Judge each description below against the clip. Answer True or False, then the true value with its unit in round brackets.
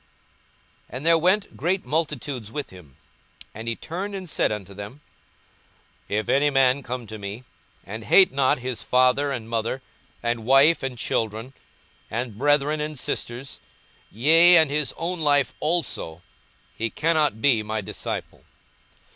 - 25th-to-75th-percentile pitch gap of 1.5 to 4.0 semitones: False (5.3 semitones)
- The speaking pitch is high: False (130 Hz)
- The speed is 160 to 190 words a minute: False (150 wpm)